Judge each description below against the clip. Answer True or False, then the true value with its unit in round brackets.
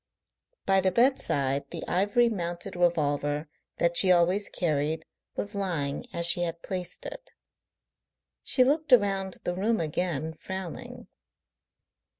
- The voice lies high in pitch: False (180 Hz)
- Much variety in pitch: False (3.8 semitones)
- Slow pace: True (125 wpm)